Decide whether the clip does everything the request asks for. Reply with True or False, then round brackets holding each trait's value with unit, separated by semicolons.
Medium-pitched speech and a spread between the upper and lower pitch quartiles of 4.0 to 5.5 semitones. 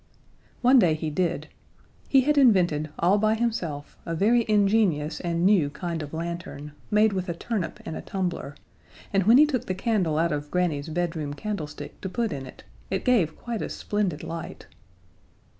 True (180 Hz; 5.2 semitones)